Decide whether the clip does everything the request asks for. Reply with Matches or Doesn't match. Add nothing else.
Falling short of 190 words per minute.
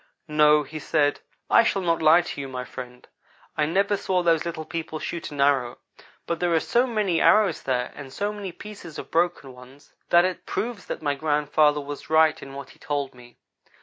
Doesn't match